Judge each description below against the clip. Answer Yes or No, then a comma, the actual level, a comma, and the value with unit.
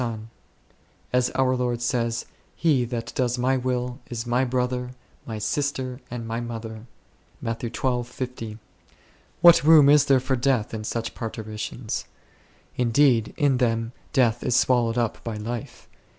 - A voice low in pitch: Yes, low, 120 Hz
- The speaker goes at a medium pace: Yes, average, 145 wpm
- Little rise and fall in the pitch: Yes, narrow, 2.0 semitones